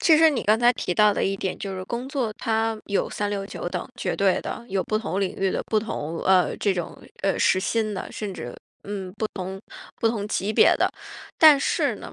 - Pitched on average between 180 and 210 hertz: Yes, high, 205 Hz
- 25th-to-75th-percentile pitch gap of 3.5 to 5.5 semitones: No, average, 2.8 semitones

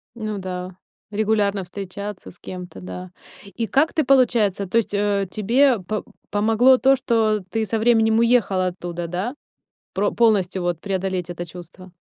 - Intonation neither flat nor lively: Yes, average, 3.6 semitones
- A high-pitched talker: Yes, high, 205 Hz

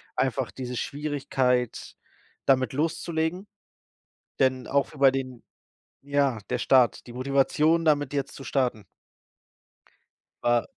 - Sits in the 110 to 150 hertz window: Yes, low, 135 Hz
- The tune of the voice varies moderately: No, narrow, 2.3 semitones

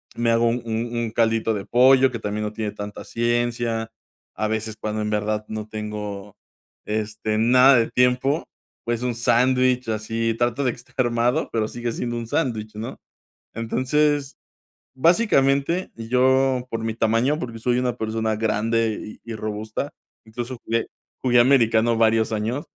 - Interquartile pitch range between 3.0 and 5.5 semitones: No, narrow, 2.4 semitones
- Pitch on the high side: No, low, 115 Hz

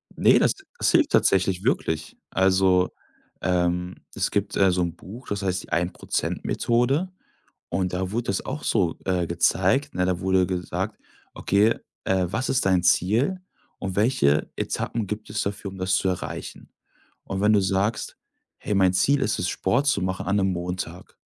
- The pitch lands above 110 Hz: No, very low, 95 Hz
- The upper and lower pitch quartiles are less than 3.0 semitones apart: Yes, narrow, 2.6 semitones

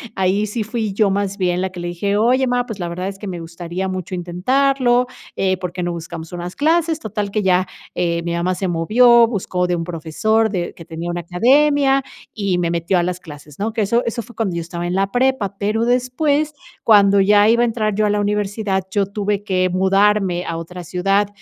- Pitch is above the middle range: Yes, high, 195 Hz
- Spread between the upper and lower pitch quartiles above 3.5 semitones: Yes, average, 3.9 semitones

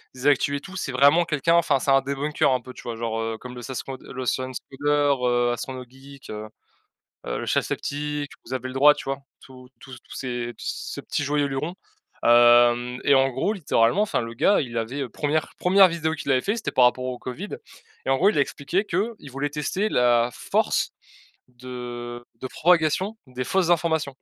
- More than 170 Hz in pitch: No, low, 135 Hz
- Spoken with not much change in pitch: No, average, 3.4 semitones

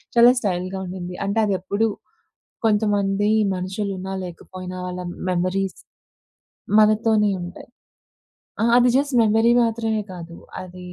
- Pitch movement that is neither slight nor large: Yes, average, 3.0 semitones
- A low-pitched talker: No, high, 195 Hz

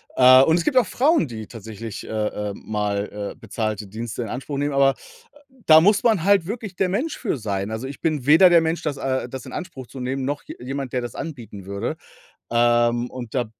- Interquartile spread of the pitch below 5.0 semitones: No, wide, 6.3 semitones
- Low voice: Yes, low, 130 Hz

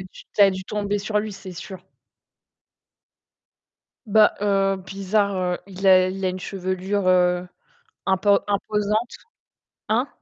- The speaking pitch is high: Yes, high, 195 Hz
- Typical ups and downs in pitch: No, narrow, 1.7 semitones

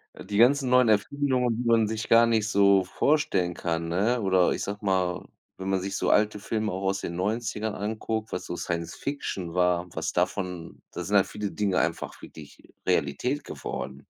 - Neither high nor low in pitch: No, low, 100 Hz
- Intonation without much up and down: No, average, 3.7 semitones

